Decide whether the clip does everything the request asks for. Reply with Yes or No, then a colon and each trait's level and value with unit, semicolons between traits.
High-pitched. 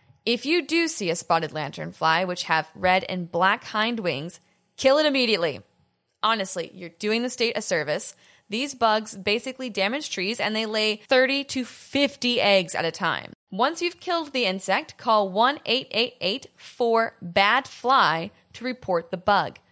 Yes: high, 215 Hz